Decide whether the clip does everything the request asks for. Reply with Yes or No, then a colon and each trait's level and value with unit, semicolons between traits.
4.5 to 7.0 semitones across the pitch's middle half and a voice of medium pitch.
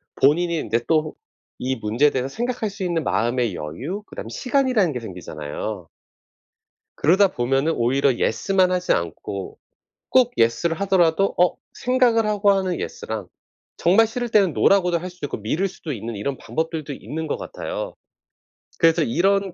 No: wide, 7.6 semitones; medium, 165 Hz